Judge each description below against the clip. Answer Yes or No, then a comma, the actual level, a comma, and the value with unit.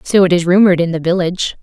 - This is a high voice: No, medium, 180 Hz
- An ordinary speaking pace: No, fast, 260 wpm